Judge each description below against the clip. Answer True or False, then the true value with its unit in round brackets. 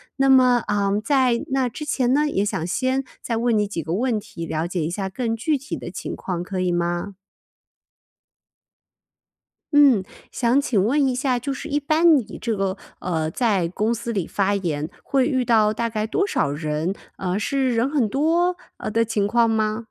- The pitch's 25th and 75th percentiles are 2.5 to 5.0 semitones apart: False (5.5 semitones)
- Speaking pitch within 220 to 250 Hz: True (225 Hz)